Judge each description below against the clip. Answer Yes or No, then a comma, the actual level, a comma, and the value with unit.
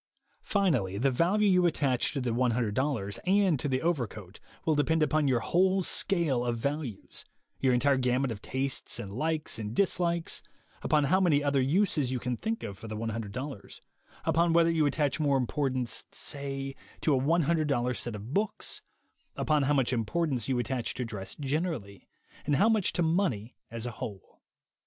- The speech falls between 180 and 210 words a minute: No, average, 170 wpm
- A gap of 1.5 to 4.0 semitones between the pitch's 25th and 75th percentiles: No, average, 5.2 semitones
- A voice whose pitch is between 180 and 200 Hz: No, low, 135 Hz